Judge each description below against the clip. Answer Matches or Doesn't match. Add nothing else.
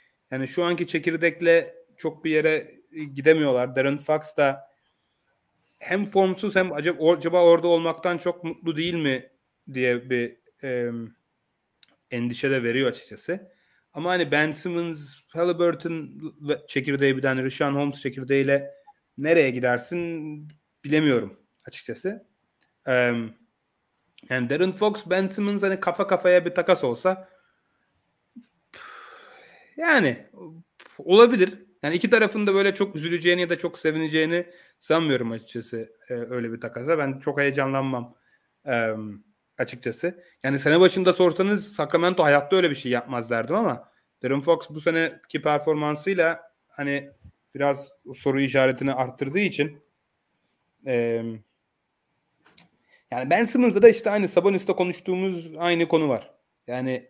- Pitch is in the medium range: Matches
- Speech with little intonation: Doesn't match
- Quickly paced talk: Doesn't match